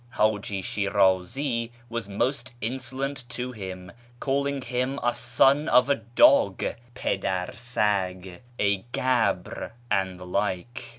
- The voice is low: Yes, low, 115 Hz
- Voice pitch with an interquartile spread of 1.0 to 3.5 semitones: No, average, 4.7 semitones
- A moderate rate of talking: No, slow, 125 wpm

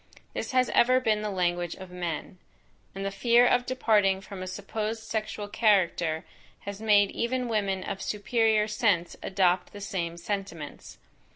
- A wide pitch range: No, average, 3.0 semitones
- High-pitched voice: Yes, high, 205 Hz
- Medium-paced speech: Yes, average, 155 wpm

